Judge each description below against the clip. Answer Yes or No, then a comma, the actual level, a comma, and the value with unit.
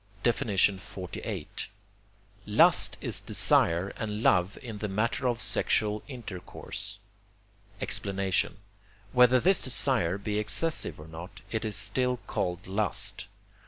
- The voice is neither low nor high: No, low, 105 Hz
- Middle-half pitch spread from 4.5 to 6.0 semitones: No, average, 3.9 semitones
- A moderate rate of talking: No, slow, 110 wpm